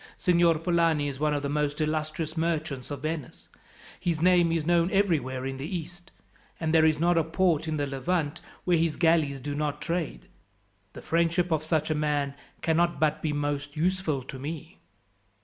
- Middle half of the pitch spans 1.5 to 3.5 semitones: Yes, narrow, 2.5 semitones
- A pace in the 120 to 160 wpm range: No, average, 185 wpm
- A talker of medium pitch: Yes, medium, 155 Hz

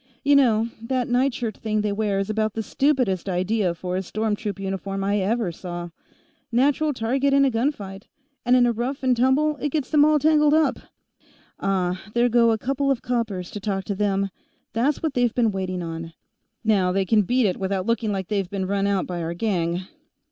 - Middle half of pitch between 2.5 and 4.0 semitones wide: No, average, 4.6 semitones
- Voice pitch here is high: Yes, high, 215 Hz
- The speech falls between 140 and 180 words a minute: No, fast, 205 wpm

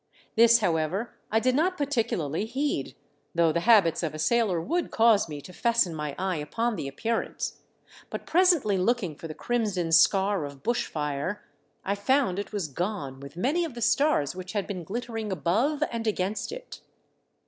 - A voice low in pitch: No, high, 205 Hz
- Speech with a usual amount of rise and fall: No, wide, 6.1 semitones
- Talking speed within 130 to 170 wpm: No, average, 180 wpm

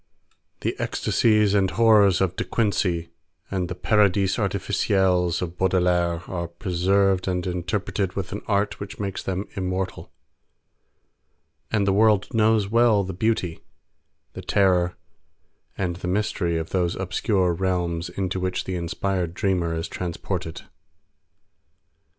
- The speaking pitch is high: No, very low, 95 Hz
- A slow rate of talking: Yes, slow, 125 wpm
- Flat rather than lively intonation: Yes, narrow, 2.2 semitones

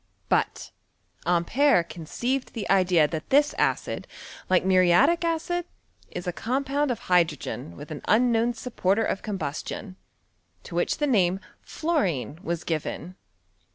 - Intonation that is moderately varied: No, wide, 7.4 semitones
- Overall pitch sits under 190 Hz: No, high, 195 Hz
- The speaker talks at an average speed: No, slow, 130 wpm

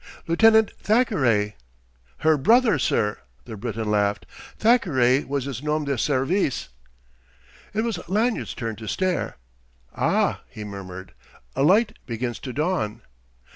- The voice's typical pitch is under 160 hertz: Yes, low, 135 Hz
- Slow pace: Yes, slow, 130 wpm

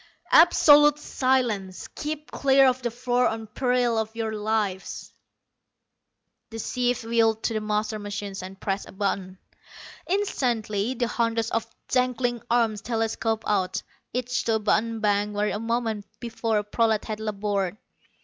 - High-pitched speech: Yes, high, 225 Hz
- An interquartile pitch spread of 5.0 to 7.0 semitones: No, average, 2.7 semitones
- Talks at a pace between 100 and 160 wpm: Yes, average, 145 wpm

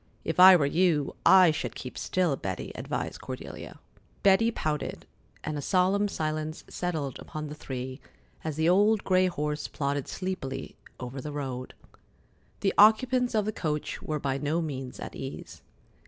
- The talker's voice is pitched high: No, medium, 155 Hz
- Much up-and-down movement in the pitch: No, average, 4.9 semitones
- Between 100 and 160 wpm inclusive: Yes, average, 155 wpm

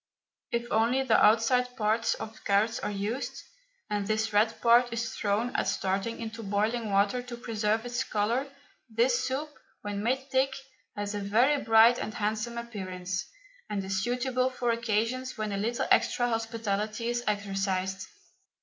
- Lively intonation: No, average, 2.8 semitones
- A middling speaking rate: Yes, average, 155 wpm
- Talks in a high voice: Yes, high, 225 Hz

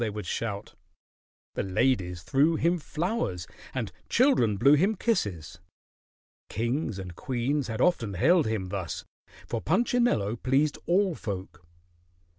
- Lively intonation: Yes, wide, 8.7 semitones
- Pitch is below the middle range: Yes, low, 120 Hz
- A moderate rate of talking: No, slow, 125 wpm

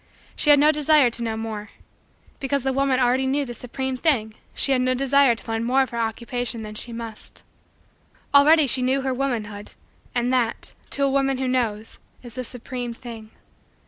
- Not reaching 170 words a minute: No, average, 190 wpm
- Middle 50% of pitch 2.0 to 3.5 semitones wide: Yes, average, 2.8 semitones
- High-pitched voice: Yes, very high, 255 Hz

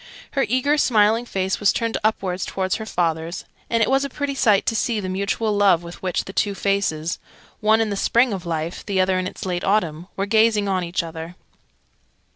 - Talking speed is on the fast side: Yes, fast, 210 wpm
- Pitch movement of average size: Yes, average, 3.6 semitones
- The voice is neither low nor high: No, high, 200 Hz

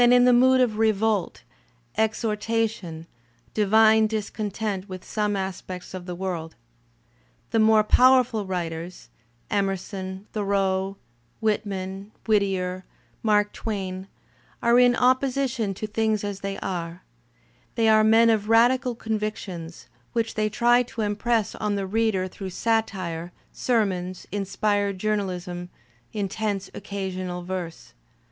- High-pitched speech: Yes, high, 205 Hz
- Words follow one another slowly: Yes, slow, 125 wpm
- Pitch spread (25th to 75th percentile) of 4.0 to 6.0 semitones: No, average, 2.8 semitones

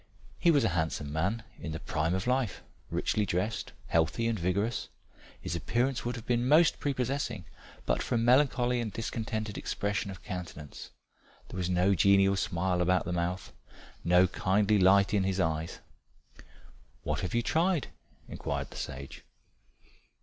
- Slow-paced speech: No, average, 155 wpm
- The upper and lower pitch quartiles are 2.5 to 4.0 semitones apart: No, average, 4.9 semitones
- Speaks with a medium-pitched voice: No, low, 100 Hz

